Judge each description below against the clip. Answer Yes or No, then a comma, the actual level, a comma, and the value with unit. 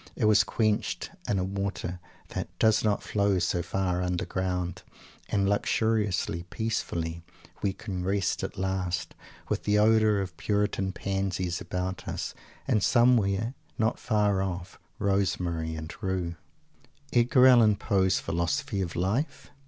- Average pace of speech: No, slow, 130 wpm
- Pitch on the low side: Yes, very low, 95 Hz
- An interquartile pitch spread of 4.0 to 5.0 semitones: No, average, 2.7 semitones